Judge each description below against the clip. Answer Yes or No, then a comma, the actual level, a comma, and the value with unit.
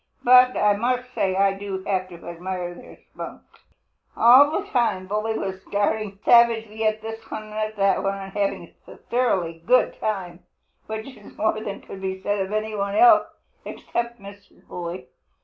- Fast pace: No, average, 170 wpm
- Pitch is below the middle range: No, high, 205 Hz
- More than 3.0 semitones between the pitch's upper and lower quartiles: No, narrow, 2.6 semitones